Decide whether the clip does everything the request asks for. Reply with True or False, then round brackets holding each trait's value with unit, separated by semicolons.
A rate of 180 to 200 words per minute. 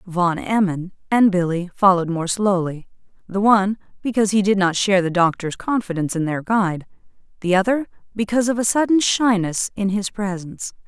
False (165 wpm)